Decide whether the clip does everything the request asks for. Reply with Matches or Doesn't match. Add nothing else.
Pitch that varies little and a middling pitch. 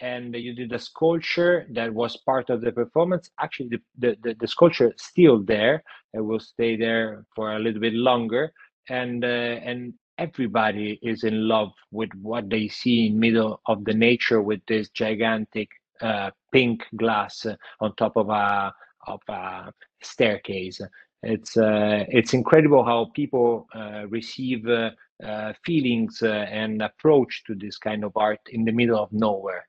Doesn't match